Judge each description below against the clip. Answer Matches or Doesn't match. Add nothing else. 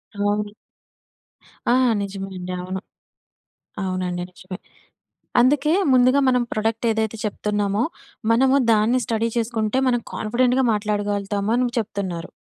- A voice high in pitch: Matches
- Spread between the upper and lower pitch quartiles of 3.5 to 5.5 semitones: Doesn't match